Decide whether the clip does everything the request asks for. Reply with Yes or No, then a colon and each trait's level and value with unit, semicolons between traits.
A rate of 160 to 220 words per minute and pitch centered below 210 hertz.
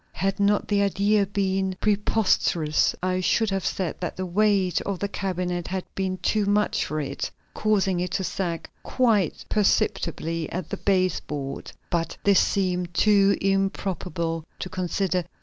No: average, 150 wpm; high, 190 Hz